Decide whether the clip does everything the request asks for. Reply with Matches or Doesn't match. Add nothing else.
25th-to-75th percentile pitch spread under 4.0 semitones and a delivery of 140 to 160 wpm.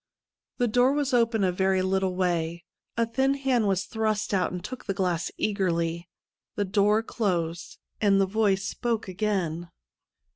Matches